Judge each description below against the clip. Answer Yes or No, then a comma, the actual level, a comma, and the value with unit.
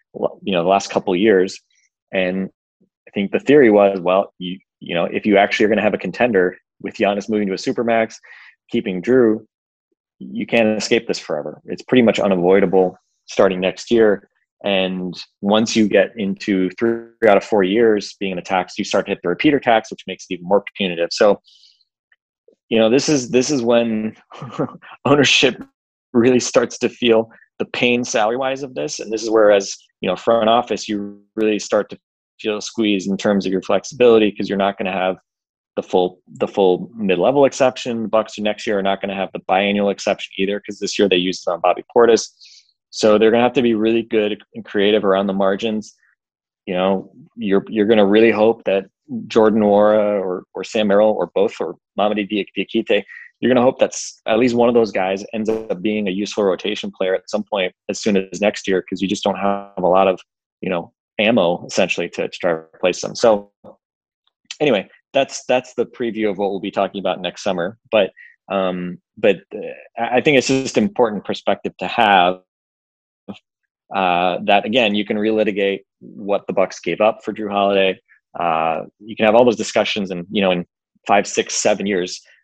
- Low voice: Yes, low, 105 Hz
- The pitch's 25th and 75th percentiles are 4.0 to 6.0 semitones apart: No, average, 2.7 semitones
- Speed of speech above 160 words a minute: Yes, average, 200 wpm